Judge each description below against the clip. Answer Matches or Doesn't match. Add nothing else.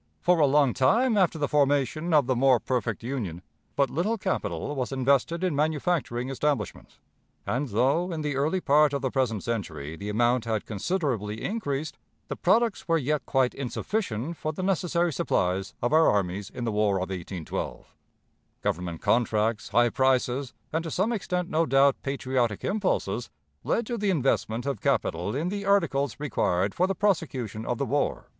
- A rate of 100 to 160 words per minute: Doesn't match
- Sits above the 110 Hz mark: Matches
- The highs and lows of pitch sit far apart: Matches